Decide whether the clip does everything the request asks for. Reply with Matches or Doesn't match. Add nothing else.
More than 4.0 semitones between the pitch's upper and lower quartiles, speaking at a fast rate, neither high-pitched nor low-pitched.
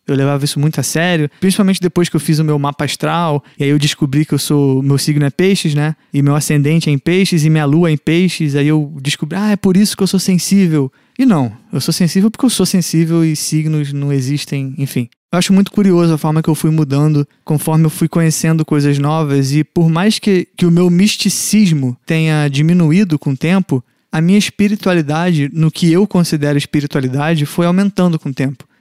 Doesn't match